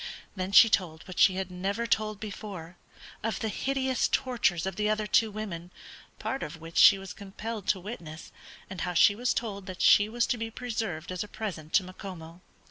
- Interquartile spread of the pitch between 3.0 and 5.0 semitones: Yes, average, 3.5 semitones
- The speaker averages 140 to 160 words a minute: No, average, 200 wpm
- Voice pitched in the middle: No, high, 200 Hz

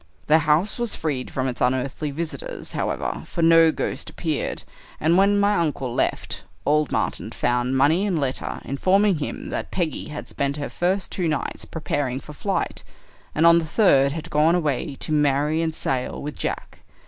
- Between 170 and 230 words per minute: Yes, average, 175 wpm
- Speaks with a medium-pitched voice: Yes, medium, 155 Hz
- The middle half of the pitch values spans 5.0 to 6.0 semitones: No, average, 3.5 semitones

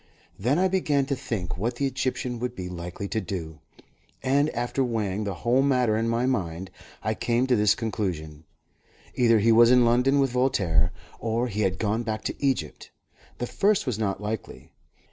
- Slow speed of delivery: No, average, 185 wpm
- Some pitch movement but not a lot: Yes, average, 4.4 semitones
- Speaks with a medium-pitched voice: No, low, 115 Hz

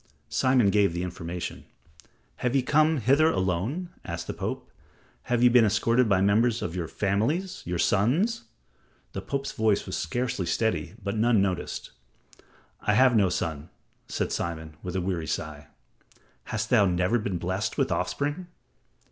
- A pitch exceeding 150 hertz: No, low, 105 Hz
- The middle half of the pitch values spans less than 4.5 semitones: No, wide, 5.4 semitones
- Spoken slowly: No, average, 155 wpm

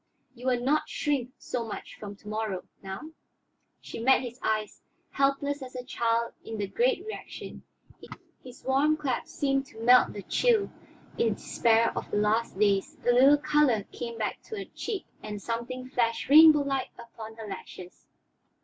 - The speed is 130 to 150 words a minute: No, average, 165 wpm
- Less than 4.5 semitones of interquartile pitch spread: Yes, average, 4.0 semitones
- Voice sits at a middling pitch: No, high, 245 Hz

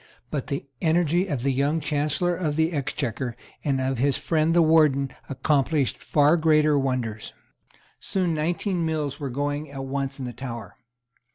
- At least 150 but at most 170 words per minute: Yes, average, 160 wpm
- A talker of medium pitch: Yes, medium, 145 Hz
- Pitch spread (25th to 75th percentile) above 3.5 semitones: No, average, 2.9 semitones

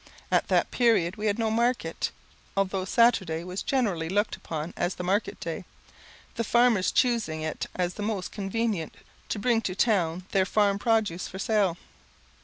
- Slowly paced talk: No, average, 165 wpm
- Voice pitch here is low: No, high, 200 Hz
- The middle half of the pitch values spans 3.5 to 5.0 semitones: Yes, average, 3.8 semitones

